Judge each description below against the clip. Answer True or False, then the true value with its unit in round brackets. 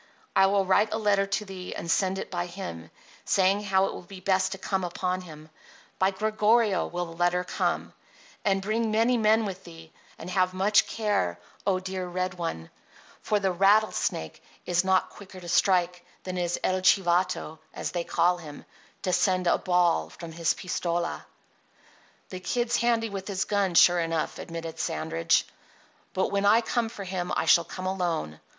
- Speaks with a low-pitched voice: False (185 Hz)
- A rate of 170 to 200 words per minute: True (180 wpm)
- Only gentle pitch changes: True (2.3 semitones)